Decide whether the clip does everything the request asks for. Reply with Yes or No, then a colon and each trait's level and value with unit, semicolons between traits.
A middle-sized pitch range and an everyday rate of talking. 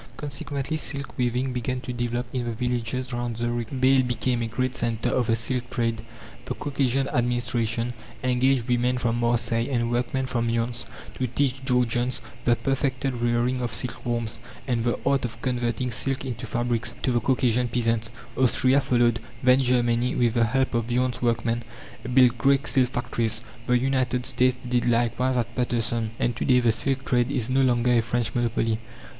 No: narrow, 1.5 semitones; average, 175 wpm